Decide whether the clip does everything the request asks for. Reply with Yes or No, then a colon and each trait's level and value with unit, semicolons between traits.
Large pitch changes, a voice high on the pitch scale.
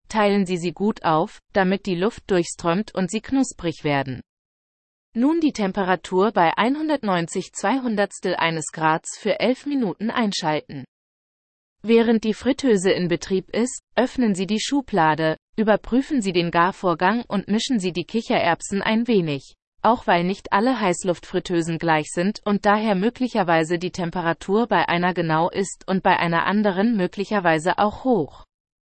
No: average, 4.5 semitones; high, 195 Hz